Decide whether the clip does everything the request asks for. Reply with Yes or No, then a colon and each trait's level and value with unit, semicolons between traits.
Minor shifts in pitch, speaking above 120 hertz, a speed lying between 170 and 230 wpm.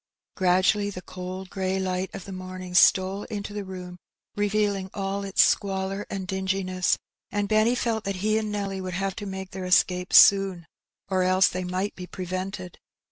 Yes: narrow, 1.5 semitones; high, 190 Hz; average, 175 wpm